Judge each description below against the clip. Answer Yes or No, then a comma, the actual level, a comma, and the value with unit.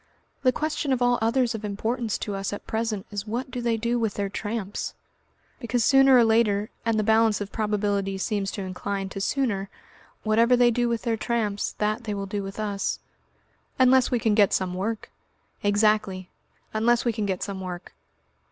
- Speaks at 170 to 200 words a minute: Yes, average, 190 wpm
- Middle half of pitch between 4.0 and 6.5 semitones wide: No, average, 2.8 semitones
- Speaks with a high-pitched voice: Yes, high, 215 Hz